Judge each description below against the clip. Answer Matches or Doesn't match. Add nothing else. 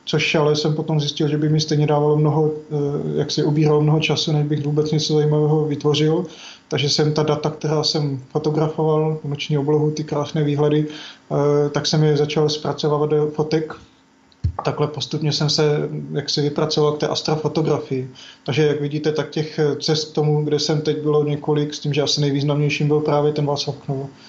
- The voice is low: Doesn't match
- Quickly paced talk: Matches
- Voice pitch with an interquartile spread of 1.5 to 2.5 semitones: Doesn't match